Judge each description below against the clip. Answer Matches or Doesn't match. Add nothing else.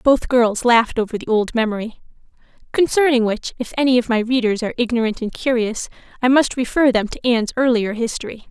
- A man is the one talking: Doesn't match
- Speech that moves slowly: Doesn't match